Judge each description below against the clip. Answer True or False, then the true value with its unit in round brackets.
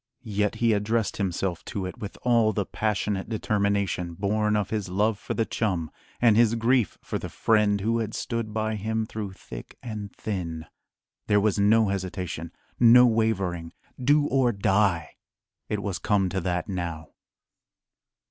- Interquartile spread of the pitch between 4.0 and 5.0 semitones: False (2.7 semitones)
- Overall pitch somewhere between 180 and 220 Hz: False (105 Hz)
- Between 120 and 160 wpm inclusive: True (155 wpm)